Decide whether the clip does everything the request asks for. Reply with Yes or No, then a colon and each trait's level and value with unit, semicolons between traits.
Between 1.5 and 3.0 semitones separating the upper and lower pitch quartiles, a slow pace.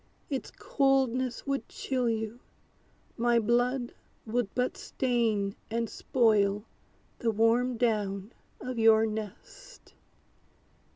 Yes: narrow, 2.5 semitones; slow, 100 wpm